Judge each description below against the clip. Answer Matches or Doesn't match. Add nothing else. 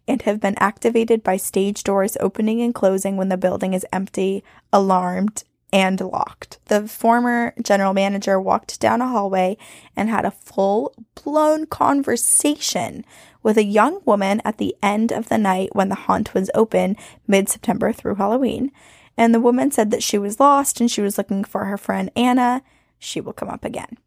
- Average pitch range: Matches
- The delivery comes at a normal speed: Matches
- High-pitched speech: Matches